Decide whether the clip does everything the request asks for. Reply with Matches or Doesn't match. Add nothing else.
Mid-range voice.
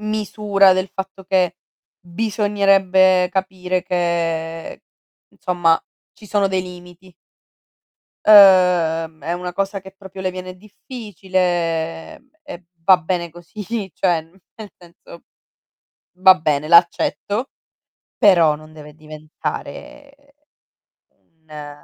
Matches